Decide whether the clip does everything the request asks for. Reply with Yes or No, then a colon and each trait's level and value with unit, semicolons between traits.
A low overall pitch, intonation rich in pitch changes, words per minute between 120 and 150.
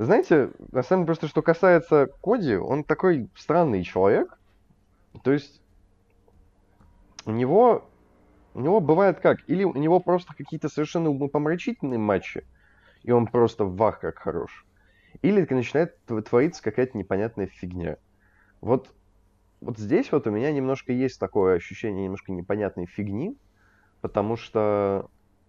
Yes: low, 110 Hz; wide, 7.6 semitones; average, 130 wpm